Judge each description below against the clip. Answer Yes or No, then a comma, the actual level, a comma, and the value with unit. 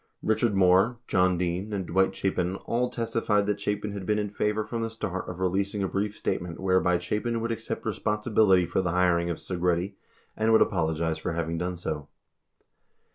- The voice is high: No, very low, 95 Hz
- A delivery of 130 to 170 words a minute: No, average, 185 wpm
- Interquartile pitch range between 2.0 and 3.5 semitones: Yes, average, 3.0 semitones